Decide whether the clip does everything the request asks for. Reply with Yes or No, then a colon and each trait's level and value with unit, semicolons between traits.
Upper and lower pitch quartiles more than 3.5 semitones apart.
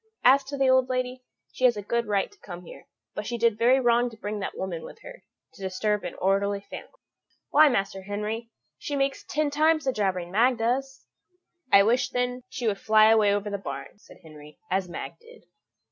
Yes: average, 4.5 semitones